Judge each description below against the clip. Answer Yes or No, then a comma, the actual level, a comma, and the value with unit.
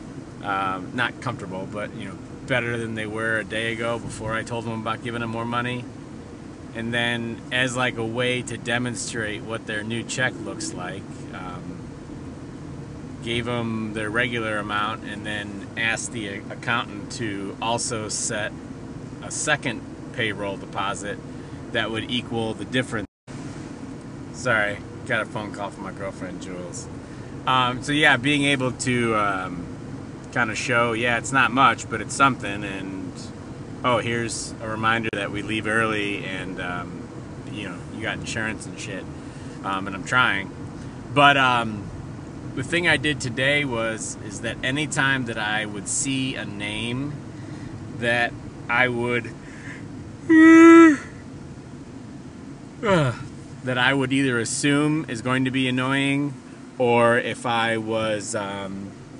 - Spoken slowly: No, average, 145 wpm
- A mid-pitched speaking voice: No, low, 120 Hz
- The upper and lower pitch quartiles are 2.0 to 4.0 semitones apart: Yes, average, 3.2 semitones